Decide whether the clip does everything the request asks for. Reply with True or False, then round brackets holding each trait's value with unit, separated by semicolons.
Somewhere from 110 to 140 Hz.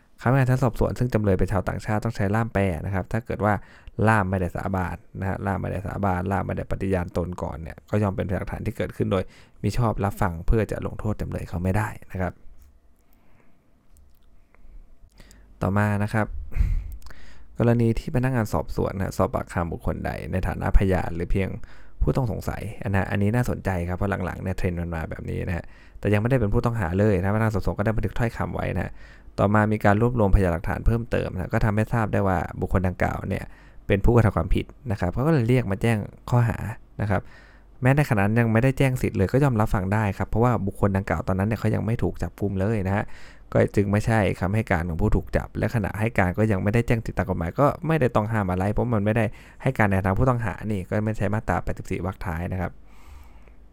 False (100 Hz)